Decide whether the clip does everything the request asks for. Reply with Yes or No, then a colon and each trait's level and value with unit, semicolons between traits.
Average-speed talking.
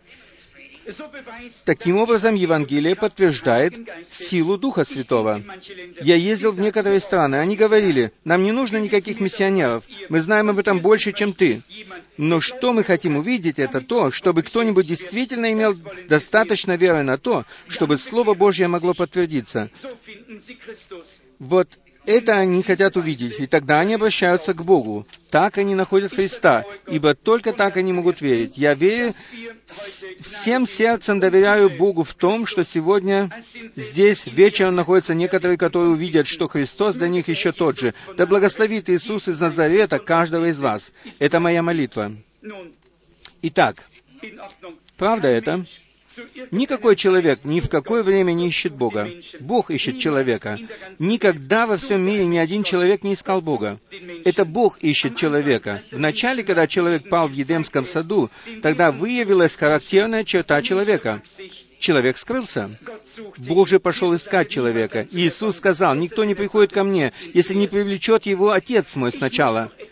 Yes: average, 140 wpm